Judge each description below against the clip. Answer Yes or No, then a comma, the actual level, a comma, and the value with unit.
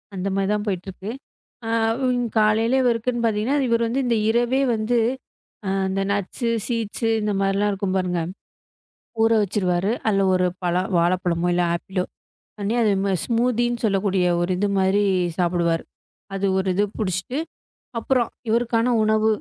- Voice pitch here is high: Yes, high, 205 Hz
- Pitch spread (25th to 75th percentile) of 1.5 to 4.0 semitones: Yes, average, 3.5 semitones